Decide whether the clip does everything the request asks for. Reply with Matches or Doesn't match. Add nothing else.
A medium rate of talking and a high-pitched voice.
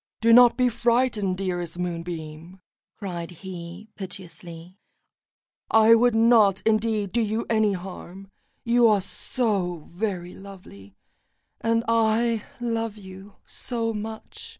Doesn't match